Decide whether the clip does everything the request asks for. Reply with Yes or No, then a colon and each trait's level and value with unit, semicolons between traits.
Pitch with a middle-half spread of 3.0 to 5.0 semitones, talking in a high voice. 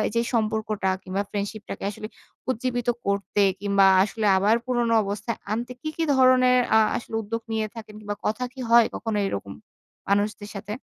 No: narrow, 2.6 semitones; high, 215 Hz